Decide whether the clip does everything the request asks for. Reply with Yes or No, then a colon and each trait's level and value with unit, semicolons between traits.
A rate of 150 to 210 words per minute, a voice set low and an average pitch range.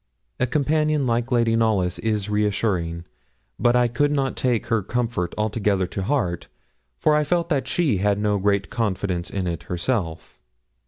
Yes: average, 160 wpm; low, 110 Hz; average, 4.9 semitones